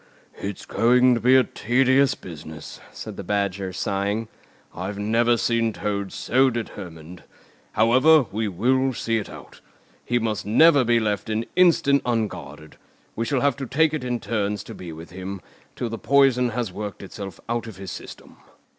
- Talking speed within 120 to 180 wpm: Yes, average, 170 wpm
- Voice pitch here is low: Yes, low, 115 Hz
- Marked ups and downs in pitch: No, average, 4.0 semitones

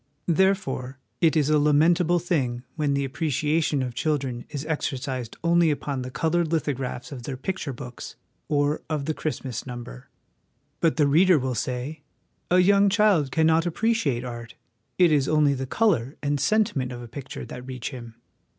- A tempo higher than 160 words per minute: Yes, average, 170 wpm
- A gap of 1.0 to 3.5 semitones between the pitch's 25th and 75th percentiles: No, average, 4.2 semitones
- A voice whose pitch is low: No, medium, 145 Hz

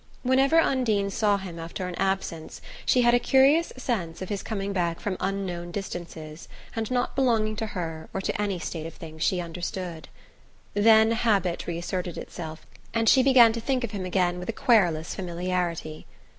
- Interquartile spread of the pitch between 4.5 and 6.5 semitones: Yes, average, 4.8 semitones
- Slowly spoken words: No, average, 175 wpm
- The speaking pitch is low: No, high, 195 Hz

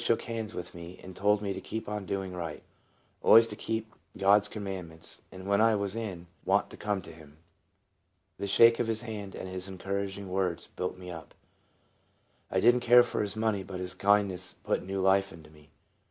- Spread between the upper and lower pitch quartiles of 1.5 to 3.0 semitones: Yes, narrow, 2.6 semitones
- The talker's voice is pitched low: Yes, low, 100 Hz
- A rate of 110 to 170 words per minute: No, average, 200 wpm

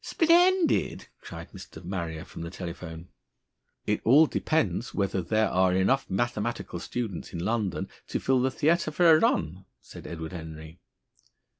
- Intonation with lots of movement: Yes, wide, 7.6 semitones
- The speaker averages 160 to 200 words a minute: No, average, 145 wpm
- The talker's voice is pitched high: No, low, 100 Hz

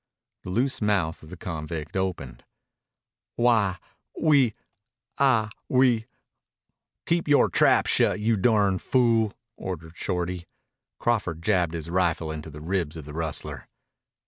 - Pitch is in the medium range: No, very low, 95 Hz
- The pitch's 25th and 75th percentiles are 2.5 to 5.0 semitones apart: No, wide, 5.6 semitones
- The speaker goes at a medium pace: No, slow, 130 wpm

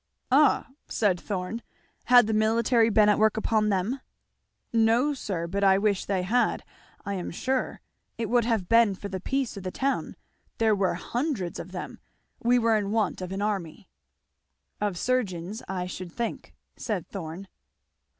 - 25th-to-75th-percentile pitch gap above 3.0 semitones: Yes, average, 3.6 semitones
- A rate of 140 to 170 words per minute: Yes, average, 165 wpm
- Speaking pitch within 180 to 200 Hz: No, high, 210 Hz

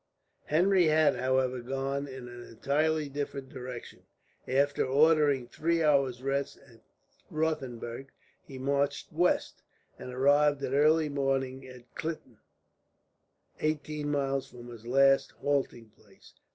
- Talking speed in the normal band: No, slow, 120 wpm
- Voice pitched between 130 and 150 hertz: Yes, low, 135 Hz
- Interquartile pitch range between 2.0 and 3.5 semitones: Yes, narrow, 2.5 semitones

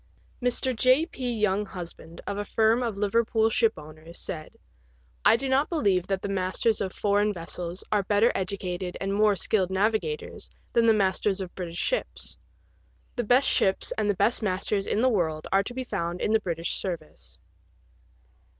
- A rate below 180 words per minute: Yes, average, 170 wpm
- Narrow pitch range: No, average, 3.6 semitones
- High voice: Yes, high, 205 Hz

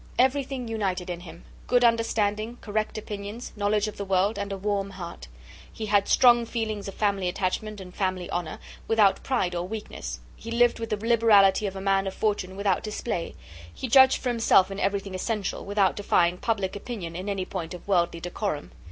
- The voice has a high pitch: Yes, high, 200 Hz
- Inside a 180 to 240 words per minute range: Yes, average, 185 wpm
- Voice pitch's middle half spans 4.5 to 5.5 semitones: No, average, 3.0 semitones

